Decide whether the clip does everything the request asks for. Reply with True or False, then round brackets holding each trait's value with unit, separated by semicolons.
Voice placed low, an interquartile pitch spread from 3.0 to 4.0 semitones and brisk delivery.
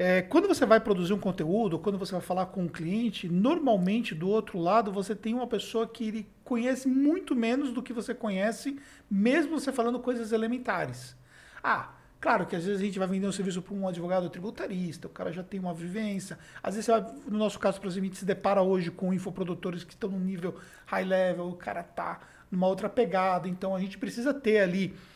False (195 Hz; 3.7 semitones; 205 wpm)